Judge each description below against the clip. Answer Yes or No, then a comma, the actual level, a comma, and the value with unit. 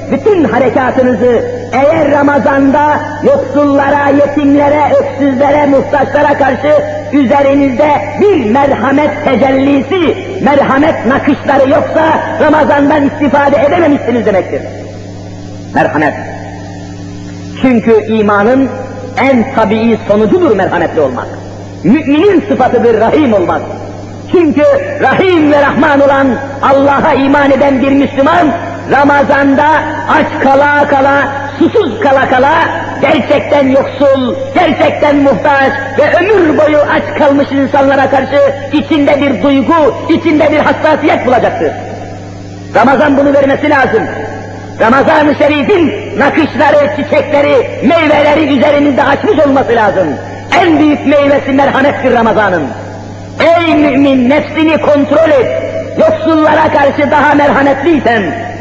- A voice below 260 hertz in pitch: No, very high, 280 Hz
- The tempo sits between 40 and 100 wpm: Yes, slow, 95 wpm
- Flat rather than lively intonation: Yes, narrow, 1.8 semitones